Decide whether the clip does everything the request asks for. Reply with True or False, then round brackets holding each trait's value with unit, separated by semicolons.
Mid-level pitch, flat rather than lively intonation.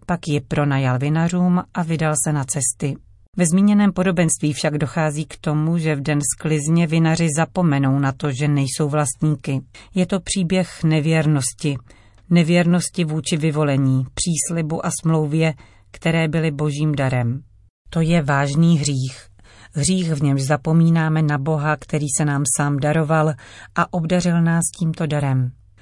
False (155 Hz; 3.0 semitones)